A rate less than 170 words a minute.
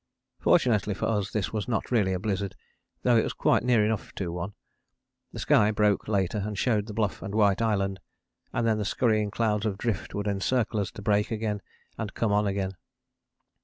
No: average, 200 wpm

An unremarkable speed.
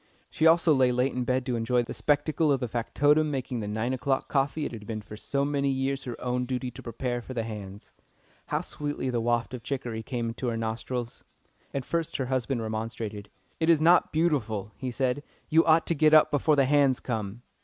No: fast, 215 wpm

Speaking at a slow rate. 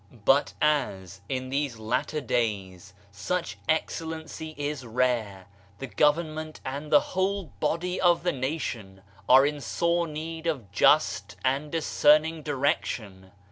Yes: slow, 130 wpm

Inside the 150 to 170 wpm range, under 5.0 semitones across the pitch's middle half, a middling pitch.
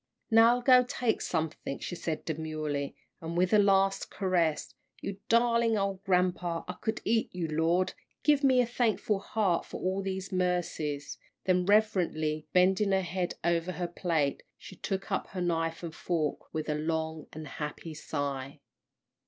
Yes: average, 160 wpm; average, 3.8 semitones; medium, 180 Hz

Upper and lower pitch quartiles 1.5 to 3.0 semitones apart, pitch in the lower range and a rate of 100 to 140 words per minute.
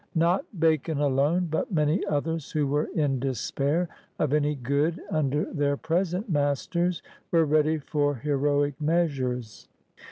No: narrow, 2.4 semitones; medium, 150 Hz; slow, 135 wpm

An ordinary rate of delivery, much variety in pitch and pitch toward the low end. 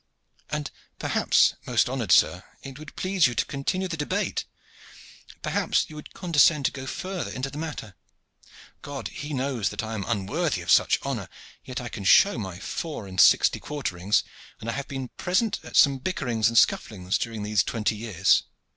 Yes: average, 180 wpm; wide, 5.8 semitones; low, 130 Hz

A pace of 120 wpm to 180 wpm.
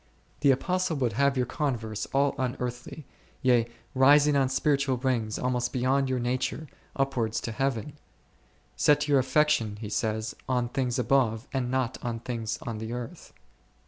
Yes: average, 155 wpm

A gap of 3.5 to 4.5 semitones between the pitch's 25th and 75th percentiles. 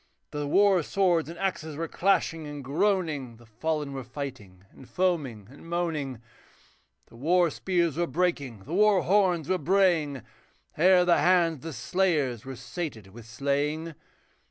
No: average, 4.9 semitones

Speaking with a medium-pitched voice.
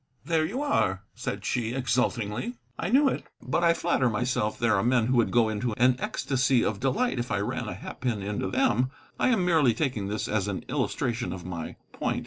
No: low, 120 Hz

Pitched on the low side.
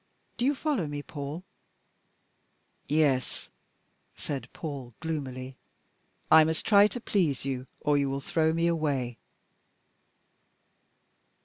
No: medium, 150 Hz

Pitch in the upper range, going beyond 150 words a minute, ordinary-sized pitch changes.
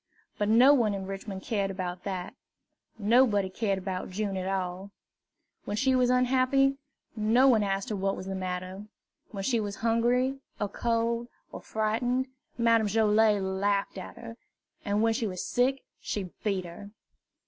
Yes: high, 210 Hz; average, 160 wpm; average, 3.4 semitones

